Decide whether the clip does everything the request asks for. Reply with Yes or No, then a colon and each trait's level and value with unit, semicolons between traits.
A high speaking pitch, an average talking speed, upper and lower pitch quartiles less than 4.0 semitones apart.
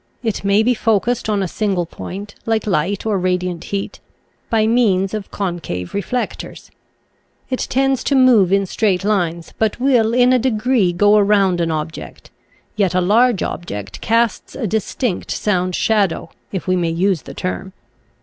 Yes: high, 200 Hz; average, 160 wpm; average, 3.6 semitones